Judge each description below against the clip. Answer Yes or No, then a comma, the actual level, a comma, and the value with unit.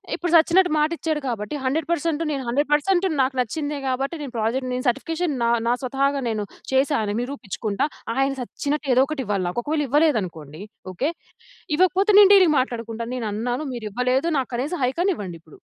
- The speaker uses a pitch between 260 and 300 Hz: Yes, very high, 270 Hz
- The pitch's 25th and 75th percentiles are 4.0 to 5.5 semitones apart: Yes, average, 4.7 semitones